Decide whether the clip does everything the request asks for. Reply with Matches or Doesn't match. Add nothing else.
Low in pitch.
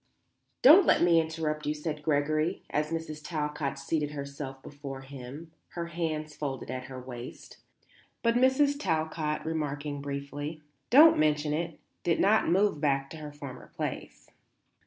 Doesn't match